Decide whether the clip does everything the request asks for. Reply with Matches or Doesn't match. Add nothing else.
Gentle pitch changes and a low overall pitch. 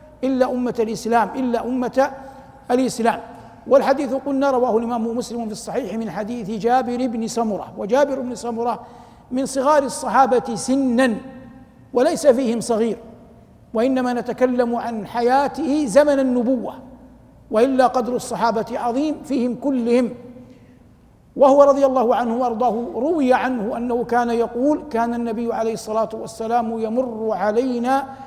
Doesn't match